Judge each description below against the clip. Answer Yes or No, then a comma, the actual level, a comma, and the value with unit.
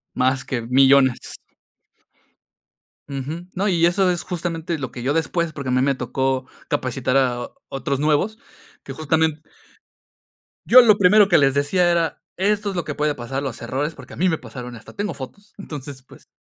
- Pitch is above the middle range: No, medium, 145 Hz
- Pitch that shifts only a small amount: No, average, 4.8 semitones